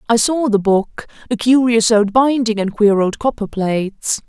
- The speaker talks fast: No, average, 170 wpm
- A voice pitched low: No, high, 225 Hz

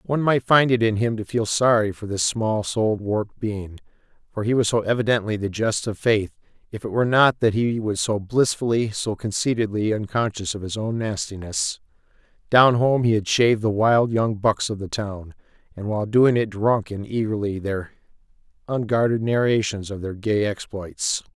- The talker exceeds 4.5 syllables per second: Yes, 5.0 syllables/s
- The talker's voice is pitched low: Yes, low, 110 Hz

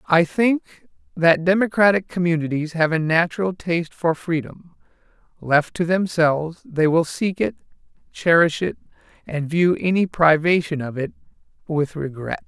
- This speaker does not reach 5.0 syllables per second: Yes, 4.6 syllables/s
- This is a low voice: No, medium, 165 Hz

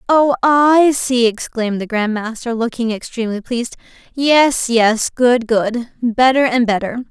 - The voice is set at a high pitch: Yes, high, 240 Hz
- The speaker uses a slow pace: Yes, slow, 125 wpm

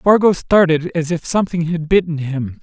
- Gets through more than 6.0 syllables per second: No, 5.0 syllables/s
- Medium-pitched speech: Yes, medium, 165 Hz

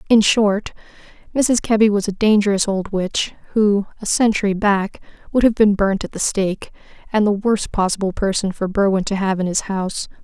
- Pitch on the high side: Yes, high, 205 Hz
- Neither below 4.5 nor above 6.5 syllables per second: Yes, 5.2 syllables/s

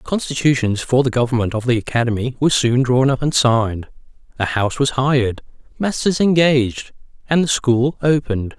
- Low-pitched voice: Yes, low, 130 Hz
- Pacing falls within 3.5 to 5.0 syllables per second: No, 5.6 syllables/s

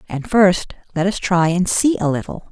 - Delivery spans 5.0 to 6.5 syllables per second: No, 4.7 syllables/s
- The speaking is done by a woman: Yes, female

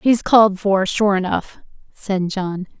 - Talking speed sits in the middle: Yes, average, 150 wpm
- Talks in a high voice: Yes, high, 195 Hz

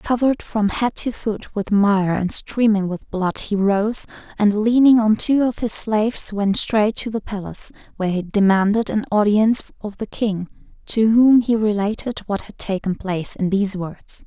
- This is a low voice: No, high, 210 Hz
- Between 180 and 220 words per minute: Yes, average, 185 wpm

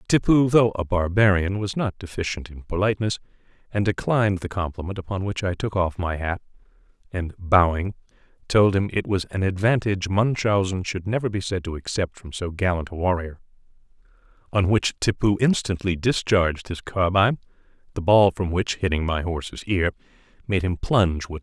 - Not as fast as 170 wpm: No, average, 175 wpm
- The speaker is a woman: No, male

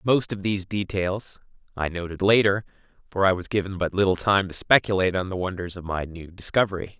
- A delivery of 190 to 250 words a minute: Yes, average, 195 wpm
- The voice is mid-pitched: No, very low, 95 Hz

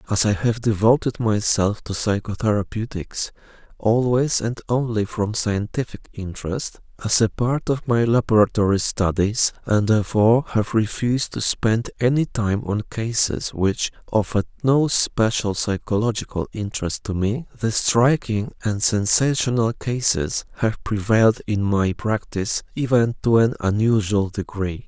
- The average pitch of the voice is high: No, low, 110 Hz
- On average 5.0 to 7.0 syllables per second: No, 4.5 syllables/s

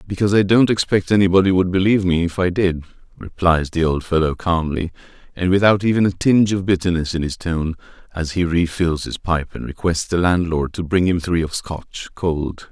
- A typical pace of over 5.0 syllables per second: Yes, 5.4 syllables/s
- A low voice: Yes, very low, 90 Hz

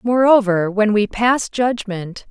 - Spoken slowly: Yes, slow, 130 wpm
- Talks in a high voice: Yes, high, 220 Hz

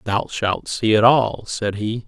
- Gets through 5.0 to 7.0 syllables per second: No, 3.7 syllables/s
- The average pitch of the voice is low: Yes, low, 110 Hz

